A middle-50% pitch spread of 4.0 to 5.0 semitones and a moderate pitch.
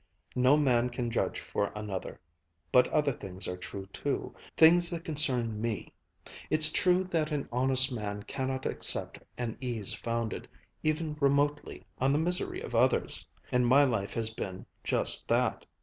No: average, 4.7 semitones; low, 130 Hz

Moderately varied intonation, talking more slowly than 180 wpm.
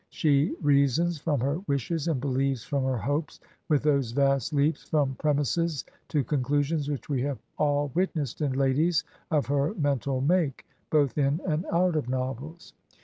No: narrow, 2.3 semitones; average, 160 wpm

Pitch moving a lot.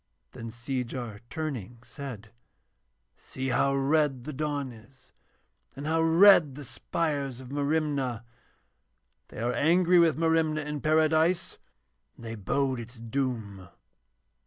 No: average, 4.5 semitones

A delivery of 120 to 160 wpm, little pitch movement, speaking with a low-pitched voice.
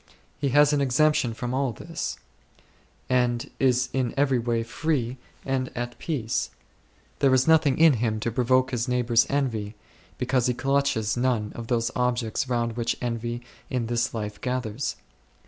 Yes: average, 155 wpm; narrow, 2.2 semitones; low, 125 Hz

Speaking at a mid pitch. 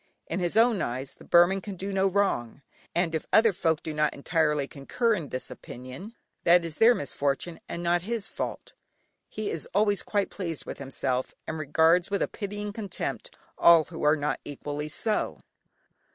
Yes: medium, 170 Hz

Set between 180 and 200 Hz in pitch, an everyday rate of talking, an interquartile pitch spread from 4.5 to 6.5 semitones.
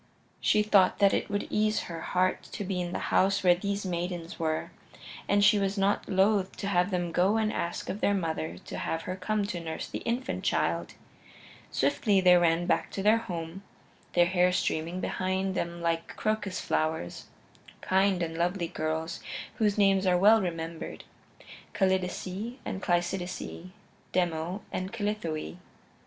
No: medium, 185 Hz; average, 160 wpm; average, 2.7 semitones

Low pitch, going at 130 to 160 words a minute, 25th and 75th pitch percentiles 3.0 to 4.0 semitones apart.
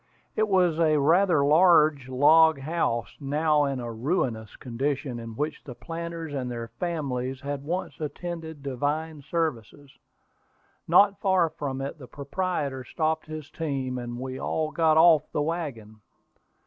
No: medium, 150 Hz; average, 145 wpm; average, 3.7 semitones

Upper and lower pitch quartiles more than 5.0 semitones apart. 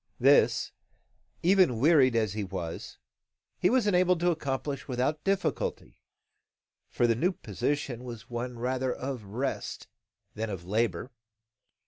Yes: wide, 5.5 semitones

